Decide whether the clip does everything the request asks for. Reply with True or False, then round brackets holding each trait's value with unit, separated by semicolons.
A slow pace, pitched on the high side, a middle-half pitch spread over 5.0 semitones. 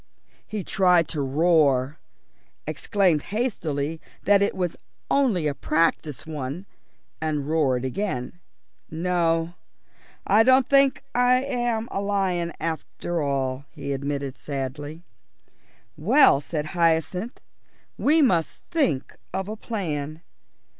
False (105 wpm; 165 Hz; 5.6 semitones)